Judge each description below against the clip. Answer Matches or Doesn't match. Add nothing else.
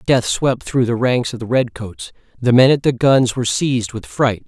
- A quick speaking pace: Matches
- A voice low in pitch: Matches